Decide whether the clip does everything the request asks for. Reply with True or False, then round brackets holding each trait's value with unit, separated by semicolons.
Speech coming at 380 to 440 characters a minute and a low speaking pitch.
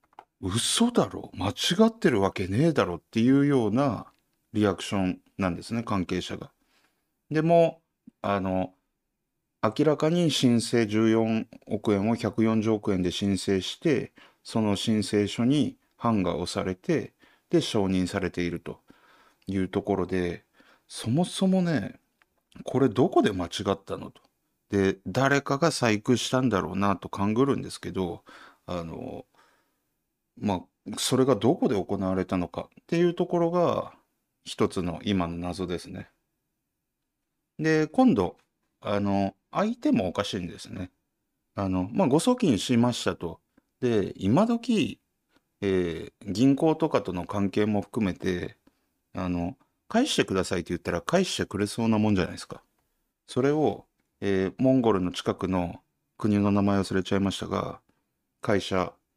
False (265 characters per minute; 105 Hz)